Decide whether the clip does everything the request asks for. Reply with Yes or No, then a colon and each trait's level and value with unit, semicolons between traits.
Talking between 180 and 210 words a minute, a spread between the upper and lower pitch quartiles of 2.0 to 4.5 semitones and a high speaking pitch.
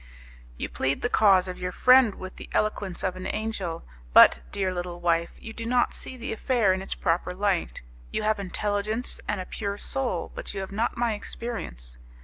Yes: average, 195 wpm; average, 3.5 semitones; high, 200 Hz